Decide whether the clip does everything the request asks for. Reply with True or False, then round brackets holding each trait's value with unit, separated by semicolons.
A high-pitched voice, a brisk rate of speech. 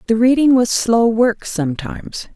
False (225 Hz; 155 wpm)